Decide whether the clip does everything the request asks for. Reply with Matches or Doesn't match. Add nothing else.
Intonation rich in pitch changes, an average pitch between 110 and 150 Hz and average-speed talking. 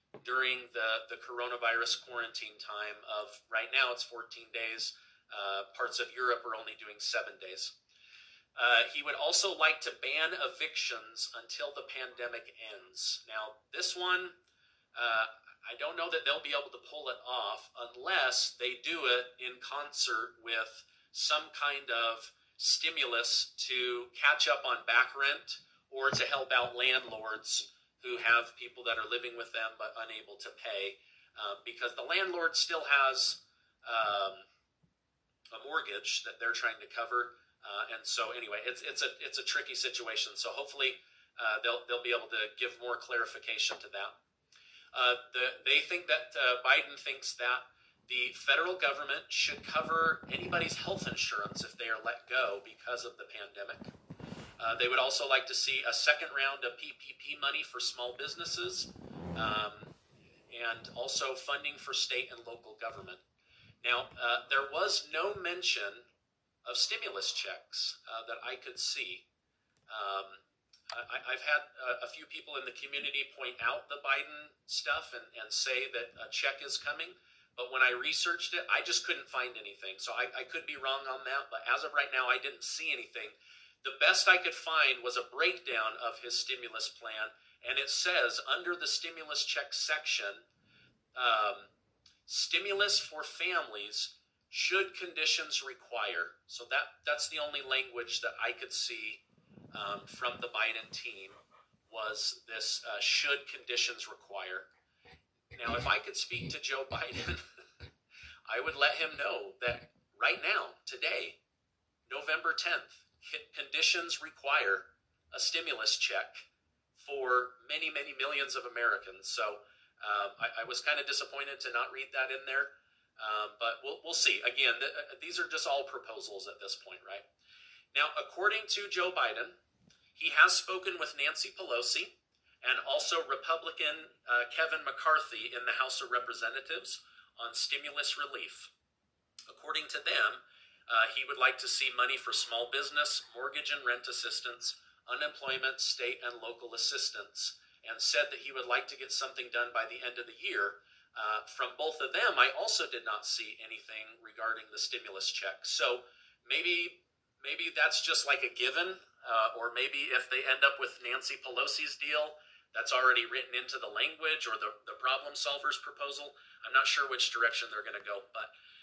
Matches